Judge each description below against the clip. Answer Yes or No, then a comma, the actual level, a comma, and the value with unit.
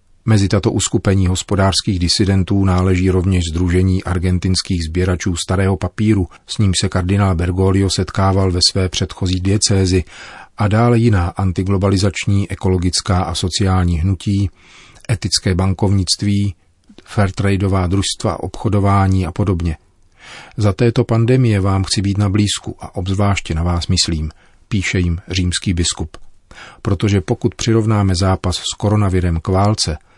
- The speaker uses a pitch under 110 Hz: Yes, very low, 95 Hz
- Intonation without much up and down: Yes, narrow, 1.8 semitones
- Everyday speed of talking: Yes, average, 125 wpm